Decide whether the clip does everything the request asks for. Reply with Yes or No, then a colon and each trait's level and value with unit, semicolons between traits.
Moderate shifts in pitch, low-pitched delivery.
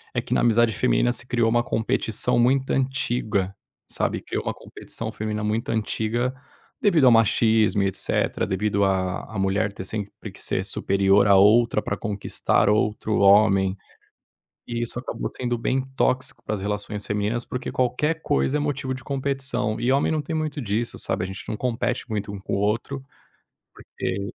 Yes: average, 3.7 semitones; low, 110 Hz